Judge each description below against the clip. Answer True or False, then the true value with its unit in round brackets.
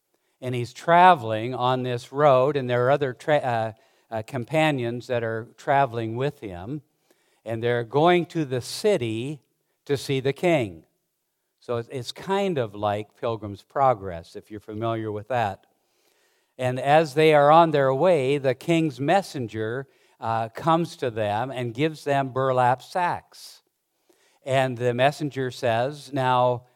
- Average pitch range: True (4.0 semitones)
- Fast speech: False (145 wpm)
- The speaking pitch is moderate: False (130 Hz)